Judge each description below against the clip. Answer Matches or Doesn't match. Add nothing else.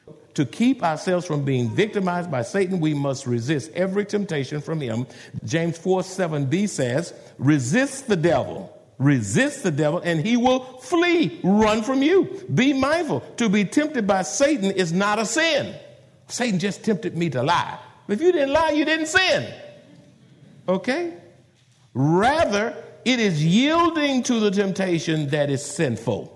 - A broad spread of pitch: Matches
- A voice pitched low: Doesn't match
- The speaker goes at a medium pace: Matches